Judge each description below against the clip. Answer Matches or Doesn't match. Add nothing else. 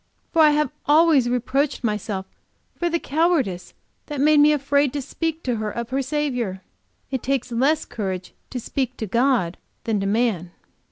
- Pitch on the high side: Matches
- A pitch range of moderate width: Matches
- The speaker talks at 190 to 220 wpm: Doesn't match